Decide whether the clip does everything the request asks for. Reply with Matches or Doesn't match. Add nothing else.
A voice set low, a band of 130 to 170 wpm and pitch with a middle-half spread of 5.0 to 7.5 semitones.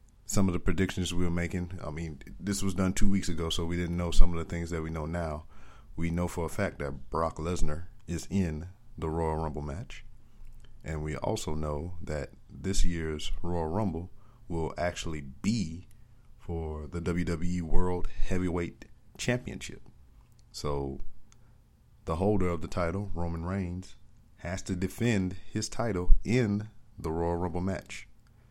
Doesn't match